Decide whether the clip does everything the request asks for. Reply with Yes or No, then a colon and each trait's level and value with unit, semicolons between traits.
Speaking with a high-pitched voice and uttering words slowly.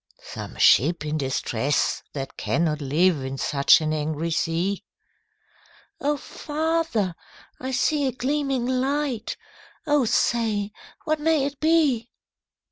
Yes: high, 230 Hz; slow, 120 wpm